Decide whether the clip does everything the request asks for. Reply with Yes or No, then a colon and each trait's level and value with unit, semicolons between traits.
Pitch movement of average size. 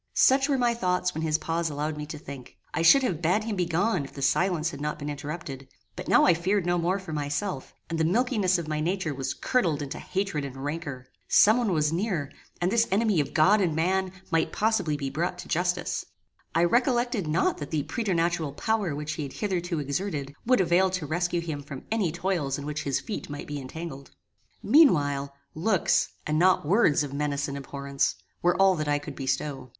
Yes: average, 4.4 semitones